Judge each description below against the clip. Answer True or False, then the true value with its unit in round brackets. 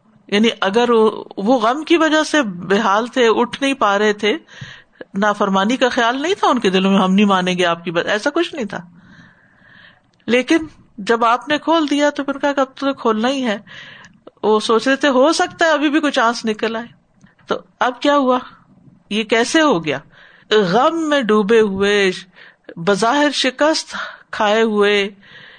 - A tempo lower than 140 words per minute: False (185 wpm)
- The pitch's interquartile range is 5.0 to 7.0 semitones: True (5.6 semitones)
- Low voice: False (230 Hz)